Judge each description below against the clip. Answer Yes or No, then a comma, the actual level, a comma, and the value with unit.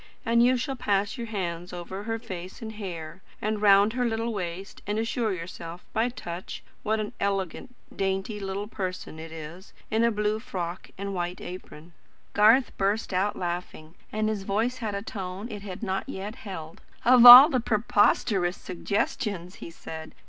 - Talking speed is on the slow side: No, average, 170 wpm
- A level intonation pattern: No, average, 3.5 semitones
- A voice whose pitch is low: No, high, 200 Hz